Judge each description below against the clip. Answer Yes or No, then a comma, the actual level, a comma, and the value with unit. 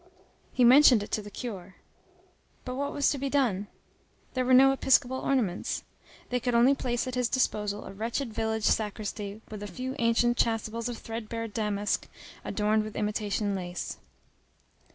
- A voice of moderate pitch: No, high, 230 Hz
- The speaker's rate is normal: Yes, average, 160 wpm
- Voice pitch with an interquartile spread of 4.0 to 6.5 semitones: No, average, 3.3 semitones